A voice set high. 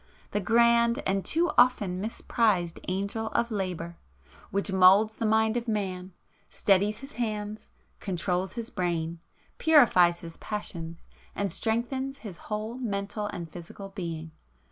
Yes: high, 205 Hz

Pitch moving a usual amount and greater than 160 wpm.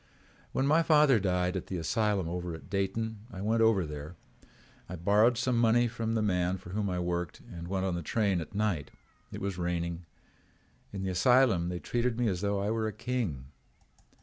Yes: average, 4.3 semitones; average, 200 wpm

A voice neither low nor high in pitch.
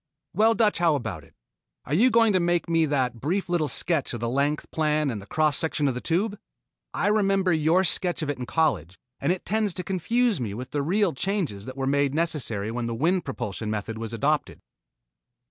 Yes: medium, 155 Hz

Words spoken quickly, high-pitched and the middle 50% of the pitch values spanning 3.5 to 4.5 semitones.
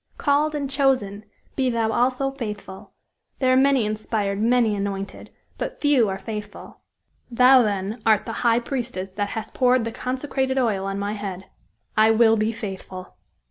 No: average, 160 wpm; high, 225 Hz; average, 4.0 semitones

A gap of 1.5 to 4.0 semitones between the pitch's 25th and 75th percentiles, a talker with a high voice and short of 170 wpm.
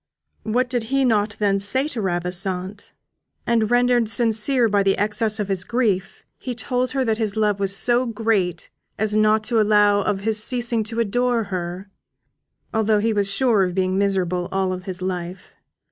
No: average, 3.2 semitones; high, 210 Hz; average, 175 wpm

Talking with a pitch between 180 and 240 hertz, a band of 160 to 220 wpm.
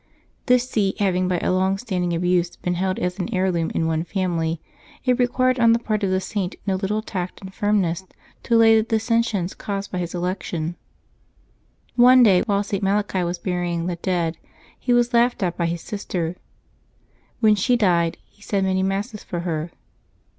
Yes: high, 190 Hz; average, 185 wpm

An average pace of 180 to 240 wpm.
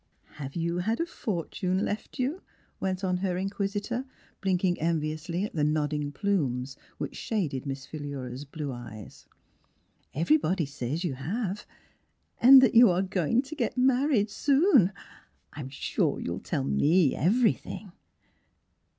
No: average, 140 wpm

